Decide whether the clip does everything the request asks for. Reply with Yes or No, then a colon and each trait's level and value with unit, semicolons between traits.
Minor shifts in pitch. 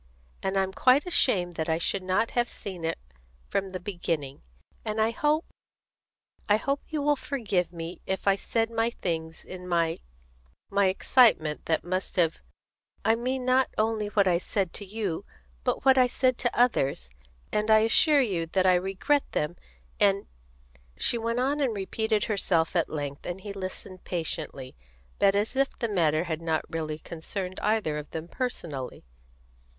No: wide, 5.4 semitones